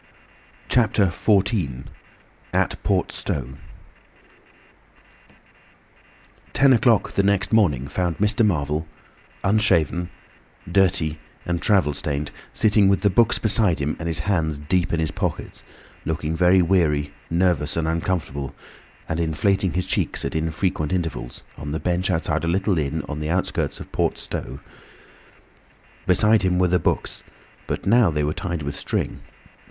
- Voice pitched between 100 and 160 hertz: No, very low, 85 Hz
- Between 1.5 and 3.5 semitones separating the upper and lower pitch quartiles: No, average, 4.2 semitones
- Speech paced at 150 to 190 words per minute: No, average, 140 wpm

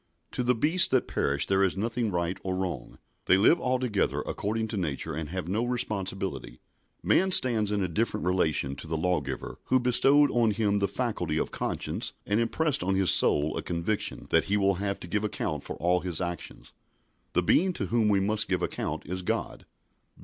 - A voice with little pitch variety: No, average, 4.6 semitones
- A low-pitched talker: Yes, low, 100 Hz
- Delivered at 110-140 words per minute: No, average, 195 wpm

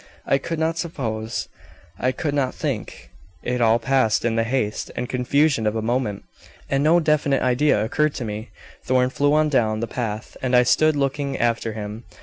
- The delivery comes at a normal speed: Yes, average, 185 wpm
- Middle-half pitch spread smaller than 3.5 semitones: No, average, 4.1 semitones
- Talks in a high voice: No, low, 125 Hz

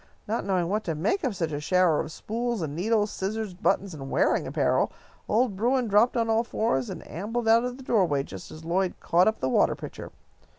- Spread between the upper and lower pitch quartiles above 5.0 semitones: Yes, wide, 5.4 semitones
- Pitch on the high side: Yes, high, 200 Hz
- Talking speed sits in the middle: No, fast, 215 wpm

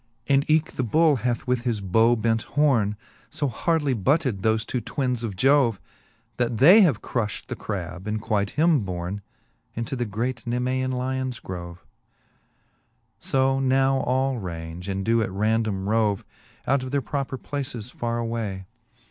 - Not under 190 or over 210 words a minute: No, average, 160 wpm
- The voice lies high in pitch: No, low, 120 Hz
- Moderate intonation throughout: Yes, average, 4.2 semitones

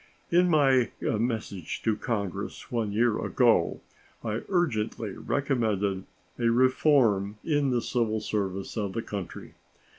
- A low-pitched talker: Yes, low, 115 Hz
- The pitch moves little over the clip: No, average, 4.0 semitones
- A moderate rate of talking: No, slow, 120 wpm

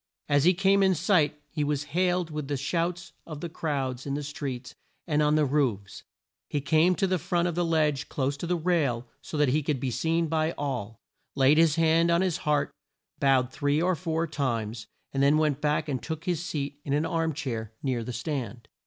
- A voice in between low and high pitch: Yes, medium, 150 Hz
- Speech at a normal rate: No, fast, 215 wpm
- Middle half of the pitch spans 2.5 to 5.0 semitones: Yes, average, 3.3 semitones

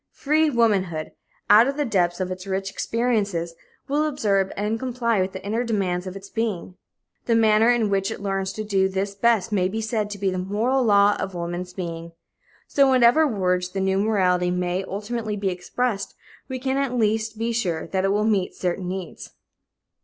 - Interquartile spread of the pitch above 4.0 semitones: No, average, 3.6 semitones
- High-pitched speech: Yes, high, 200 Hz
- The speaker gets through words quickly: No, average, 195 wpm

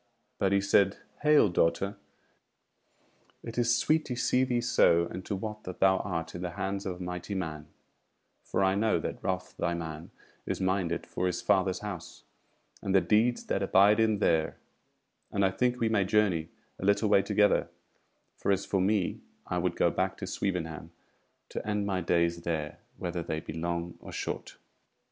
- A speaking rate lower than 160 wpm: No, average, 180 wpm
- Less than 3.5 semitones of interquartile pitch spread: Yes, average, 3.1 semitones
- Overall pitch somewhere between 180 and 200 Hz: No, very low, 95 Hz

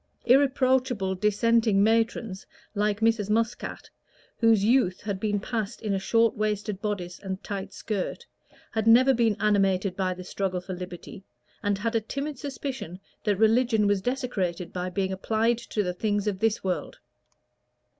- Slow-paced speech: No, average, 155 wpm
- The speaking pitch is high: Yes, high, 210 Hz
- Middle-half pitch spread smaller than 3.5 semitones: Yes, average, 3.1 semitones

